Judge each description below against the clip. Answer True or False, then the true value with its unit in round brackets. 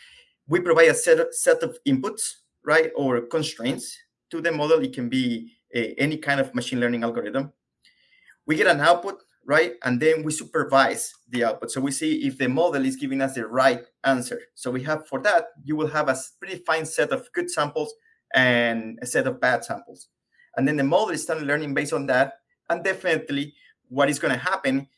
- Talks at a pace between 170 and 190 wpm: False (205 wpm)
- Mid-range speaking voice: True (155 Hz)